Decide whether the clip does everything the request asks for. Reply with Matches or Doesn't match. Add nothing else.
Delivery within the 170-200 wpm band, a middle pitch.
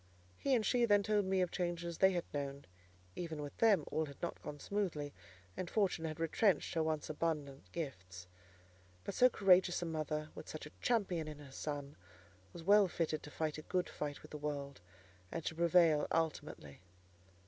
Matches